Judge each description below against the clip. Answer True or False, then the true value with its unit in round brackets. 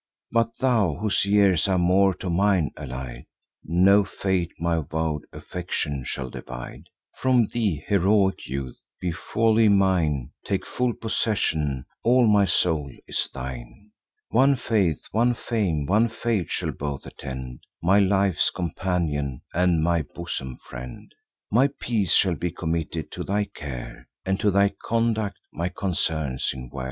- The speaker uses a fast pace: False (140 wpm)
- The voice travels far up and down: True (5.8 semitones)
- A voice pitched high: False (90 Hz)